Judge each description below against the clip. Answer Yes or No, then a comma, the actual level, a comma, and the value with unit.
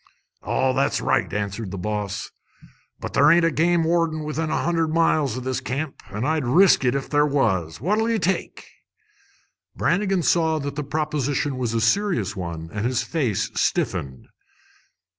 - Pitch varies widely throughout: Yes, wide, 6.4 semitones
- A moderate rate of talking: Yes, average, 170 wpm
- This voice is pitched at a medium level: Yes, medium, 145 Hz